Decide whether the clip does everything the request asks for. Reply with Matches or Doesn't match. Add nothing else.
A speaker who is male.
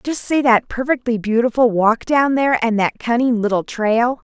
Doesn't match